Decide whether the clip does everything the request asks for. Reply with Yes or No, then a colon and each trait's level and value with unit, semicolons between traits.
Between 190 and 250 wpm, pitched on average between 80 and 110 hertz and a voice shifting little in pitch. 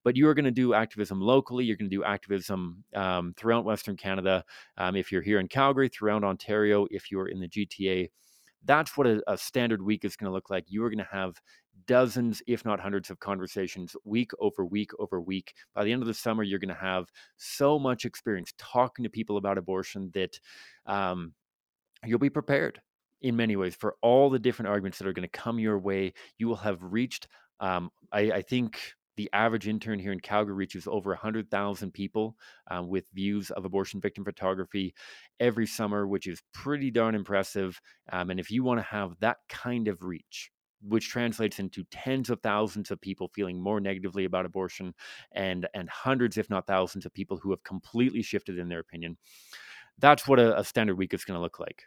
No: fast, 205 wpm; low, 100 Hz; average, 3.2 semitones